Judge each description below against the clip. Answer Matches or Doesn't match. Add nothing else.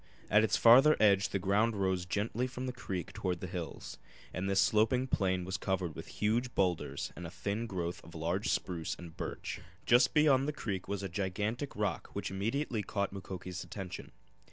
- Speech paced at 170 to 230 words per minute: Matches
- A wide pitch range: Doesn't match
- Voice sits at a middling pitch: Doesn't match